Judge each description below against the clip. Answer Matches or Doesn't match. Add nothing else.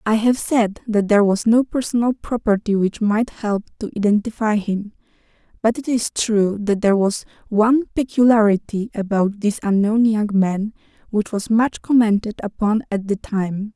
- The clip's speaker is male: Doesn't match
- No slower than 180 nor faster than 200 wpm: Doesn't match